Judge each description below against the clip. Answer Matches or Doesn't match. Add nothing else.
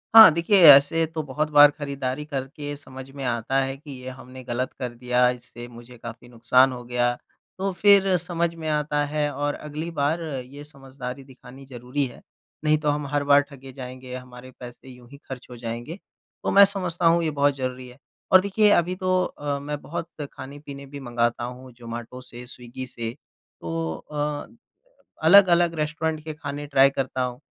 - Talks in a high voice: Doesn't match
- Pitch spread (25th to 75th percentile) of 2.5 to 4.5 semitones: Matches